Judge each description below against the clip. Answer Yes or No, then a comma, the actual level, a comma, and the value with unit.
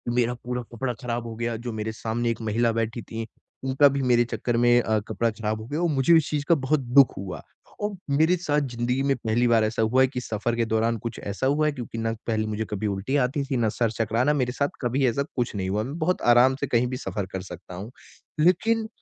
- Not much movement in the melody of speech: No, average, 3.3 semitones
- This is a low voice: Yes, low, 120 Hz